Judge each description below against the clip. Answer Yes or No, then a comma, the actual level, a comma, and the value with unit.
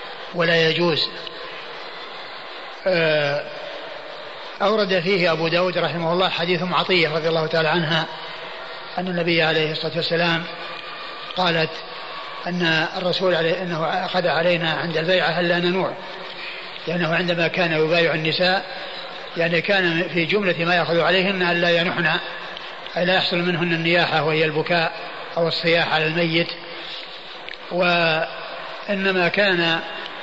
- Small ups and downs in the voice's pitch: Yes, narrow, 1.6 semitones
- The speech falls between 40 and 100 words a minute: No, average, 120 wpm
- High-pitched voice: No, medium, 170 Hz